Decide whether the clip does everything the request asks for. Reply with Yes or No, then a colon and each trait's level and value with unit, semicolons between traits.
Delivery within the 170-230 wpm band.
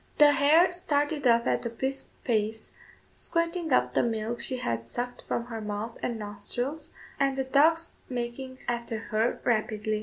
No: average, 160 wpm